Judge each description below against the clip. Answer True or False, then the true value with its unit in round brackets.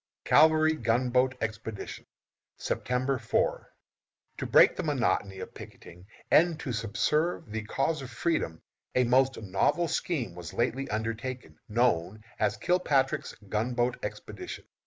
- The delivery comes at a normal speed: False (120 wpm)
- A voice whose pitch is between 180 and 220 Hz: False (125 Hz)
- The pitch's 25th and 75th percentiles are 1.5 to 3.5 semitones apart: False (4.1 semitones)